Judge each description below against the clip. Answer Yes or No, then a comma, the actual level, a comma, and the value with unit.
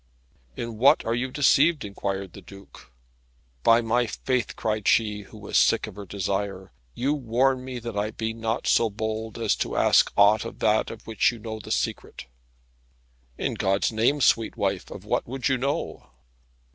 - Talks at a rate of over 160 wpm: Yes, average, 180 wpm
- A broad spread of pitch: No, average, 2.9 semitones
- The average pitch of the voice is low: Yes, low, 110 Hz